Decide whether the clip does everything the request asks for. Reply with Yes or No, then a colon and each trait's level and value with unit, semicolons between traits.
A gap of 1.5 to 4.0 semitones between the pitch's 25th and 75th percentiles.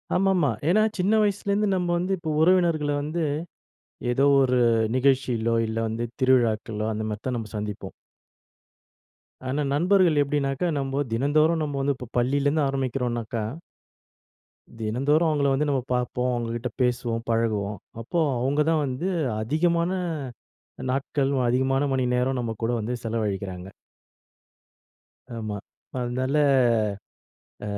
No: average, 4.6 semitones